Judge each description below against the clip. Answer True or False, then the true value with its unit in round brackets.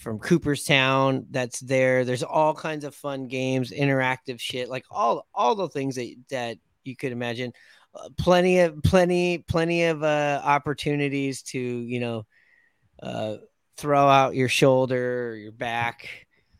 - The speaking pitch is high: False (135 Hz)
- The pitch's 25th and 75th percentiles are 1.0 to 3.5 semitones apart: True (2.8 semitones)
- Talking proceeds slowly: False (150 wpm)